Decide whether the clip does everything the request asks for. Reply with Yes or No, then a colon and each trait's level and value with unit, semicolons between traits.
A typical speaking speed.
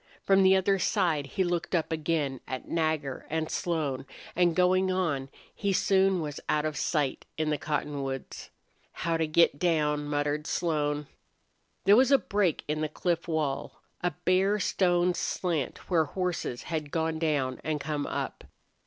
Yes: average, 160 wpm